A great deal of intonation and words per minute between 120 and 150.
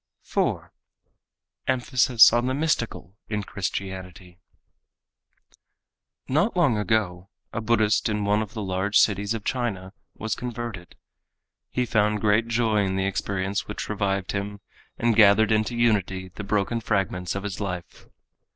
No: average, 2.9 semitones; slow, 135 wpm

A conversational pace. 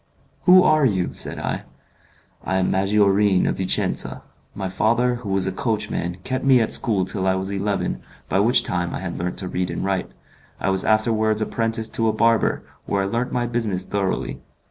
Yes: average, 190 wpm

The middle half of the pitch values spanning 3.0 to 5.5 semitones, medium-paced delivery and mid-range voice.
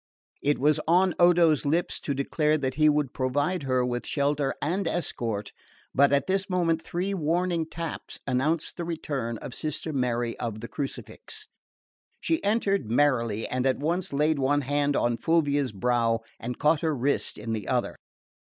Yes: average, 4.7 semitones; average, 165 wpm; medium, 145 Hz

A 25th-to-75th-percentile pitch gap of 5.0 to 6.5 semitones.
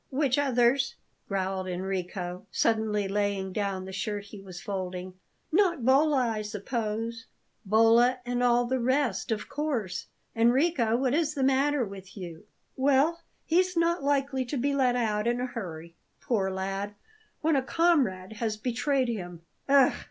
Yes: wide, 5.6 semitones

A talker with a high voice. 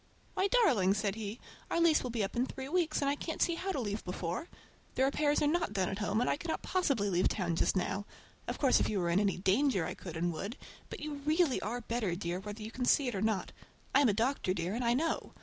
Yes: high, 225 Hz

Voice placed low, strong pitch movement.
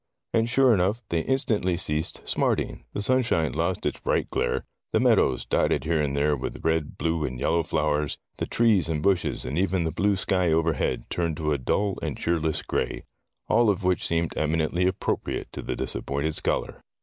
No: very low, 85 Hz; average, 3.8 semitones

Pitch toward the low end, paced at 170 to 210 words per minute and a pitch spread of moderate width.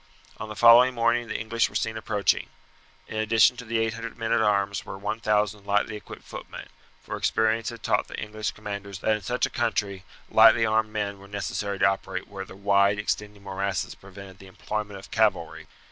No: low, 105 Hz; average, 190 wpm; narrow, 2.0 semitones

